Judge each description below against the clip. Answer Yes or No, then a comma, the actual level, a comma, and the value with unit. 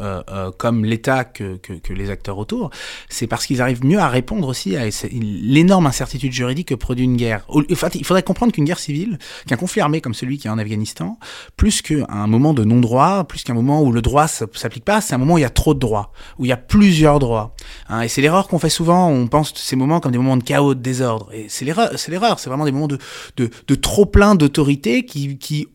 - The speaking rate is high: Yes, fast, 250 wpm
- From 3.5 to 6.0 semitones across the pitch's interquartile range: Yes, average, 4.9 semitones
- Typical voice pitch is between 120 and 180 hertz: Yes, low, 130 Hz